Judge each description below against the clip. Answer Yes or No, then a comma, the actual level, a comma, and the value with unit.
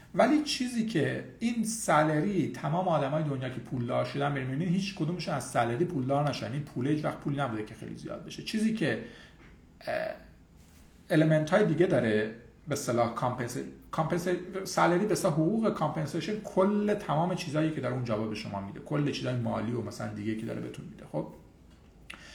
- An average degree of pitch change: No, wide, 8.0 semitones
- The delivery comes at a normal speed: No, fast, 165 wpm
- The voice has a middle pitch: Yes, medium, 145 Hz